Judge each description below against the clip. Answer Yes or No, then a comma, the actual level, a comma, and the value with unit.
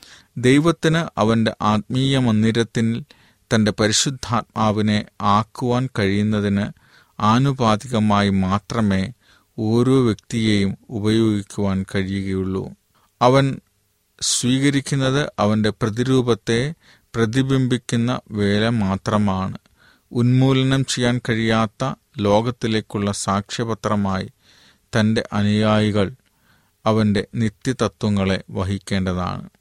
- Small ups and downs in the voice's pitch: No, average, 3.1 semitones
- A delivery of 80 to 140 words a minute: No, average, 65 wpm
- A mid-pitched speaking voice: No, low, 110 Hz